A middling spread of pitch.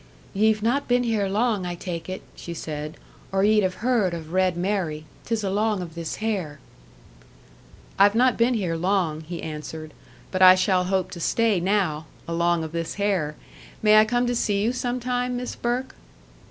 Yes: average, 4.6 semitones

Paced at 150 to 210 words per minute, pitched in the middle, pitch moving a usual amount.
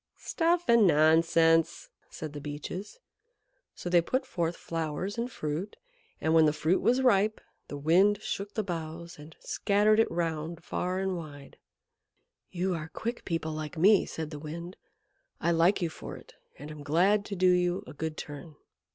Yes: average, 170 wpm; medium, 170 Hz; average, 4.0 semitones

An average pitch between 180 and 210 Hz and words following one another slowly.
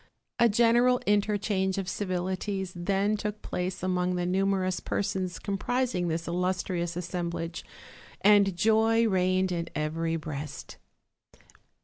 Yes: medium, 185 Hz; slow, 115 wpm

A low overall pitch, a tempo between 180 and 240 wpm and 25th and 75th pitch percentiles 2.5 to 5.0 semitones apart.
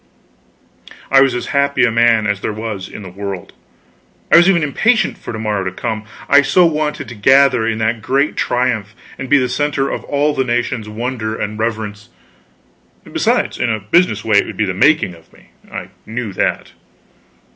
Yes: low, 115 Hz; average, 190 wpm; average, 4.4 semitones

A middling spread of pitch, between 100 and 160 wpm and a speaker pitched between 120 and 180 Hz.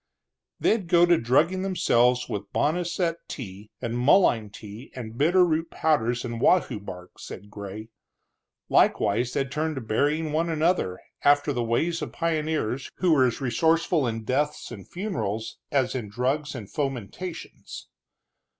No: wide, 6.1 semitones; average, 145 wpm; low, 135 Hz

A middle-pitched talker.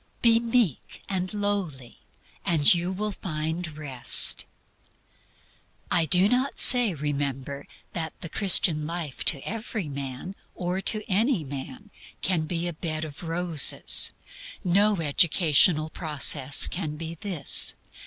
Yes: medium, 170 Hz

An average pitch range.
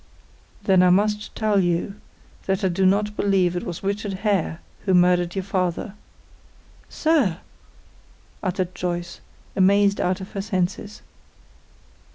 No: narrow, 2.1 semitones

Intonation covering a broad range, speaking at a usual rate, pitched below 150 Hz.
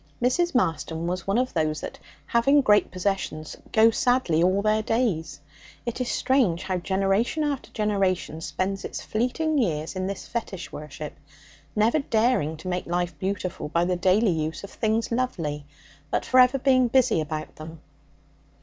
No: wide, 6.3 semitones; average, 160 wpm; high, 195 Hz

